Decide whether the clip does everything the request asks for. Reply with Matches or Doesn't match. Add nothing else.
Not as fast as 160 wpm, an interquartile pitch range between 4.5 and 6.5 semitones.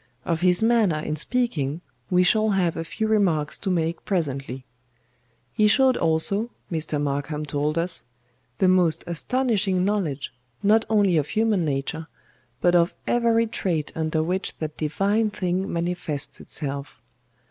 Matches